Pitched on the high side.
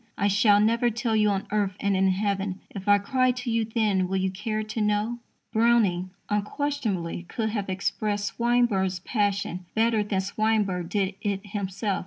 Yes: high, 205 Hz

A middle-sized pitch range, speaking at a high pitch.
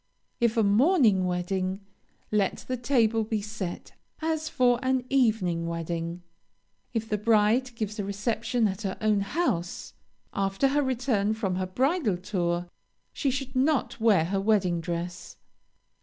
Yes: average, 5.0 semitones; high, 215 Hz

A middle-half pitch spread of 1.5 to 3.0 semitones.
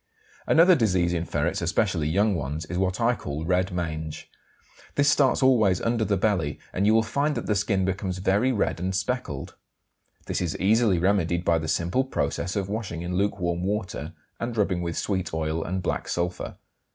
No: average, 3.9 semitones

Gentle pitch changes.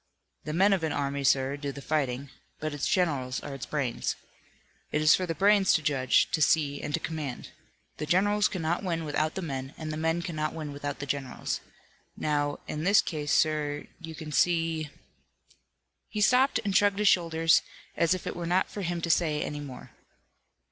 No: average, 3.2 semitones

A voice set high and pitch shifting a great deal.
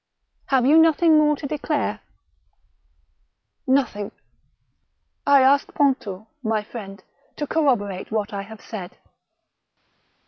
Yes: very high, 260 Hz; wide, 5.8 semitones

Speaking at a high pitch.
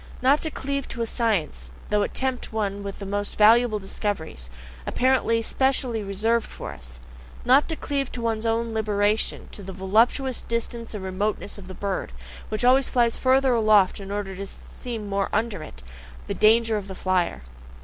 Yes: high, 215 Hz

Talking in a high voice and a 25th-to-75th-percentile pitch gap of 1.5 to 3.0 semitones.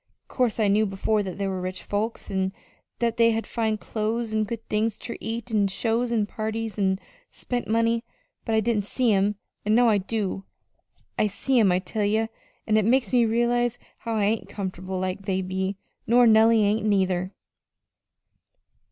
Yes: high, 215 Hz; average, 2.7 semitones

